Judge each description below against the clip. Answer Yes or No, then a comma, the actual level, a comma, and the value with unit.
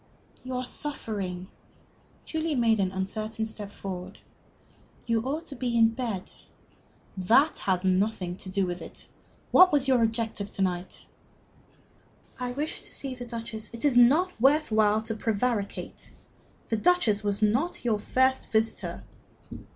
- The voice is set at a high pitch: Yes, high, 225 Hz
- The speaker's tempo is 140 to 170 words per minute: Yes, average, 150 wpm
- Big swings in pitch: No, average, 4.1 semitones